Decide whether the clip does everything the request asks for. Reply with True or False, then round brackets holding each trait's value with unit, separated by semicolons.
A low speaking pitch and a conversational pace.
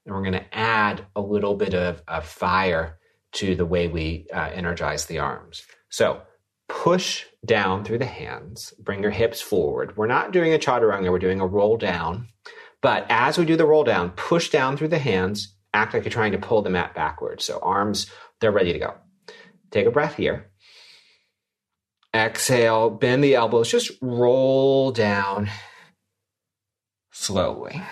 True (115 Hz; 170 wpm)